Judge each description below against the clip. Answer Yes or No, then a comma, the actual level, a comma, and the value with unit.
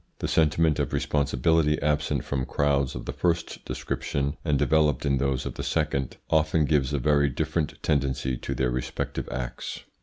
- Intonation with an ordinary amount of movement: No, narrow, 2.2 semitones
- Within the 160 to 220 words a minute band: Yes, average, 170 wpm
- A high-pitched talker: No, very low, 70 Hz